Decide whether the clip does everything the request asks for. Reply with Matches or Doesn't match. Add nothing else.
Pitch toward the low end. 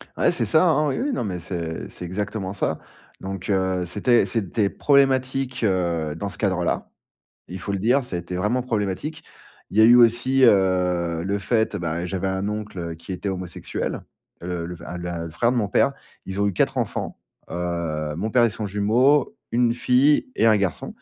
Matches